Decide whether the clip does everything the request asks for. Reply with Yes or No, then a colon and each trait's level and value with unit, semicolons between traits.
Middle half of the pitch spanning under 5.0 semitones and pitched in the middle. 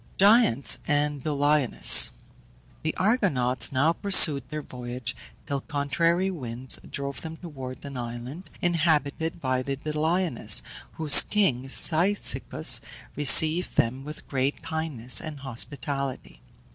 Yes: average, 3.8 semitones; medium, 145 Hz